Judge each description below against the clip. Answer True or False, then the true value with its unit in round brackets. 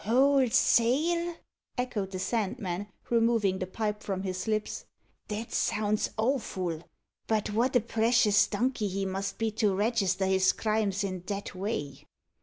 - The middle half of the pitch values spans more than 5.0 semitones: False (3.3 semitones)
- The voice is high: True (210 Hz)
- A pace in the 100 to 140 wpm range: True (135 wpm)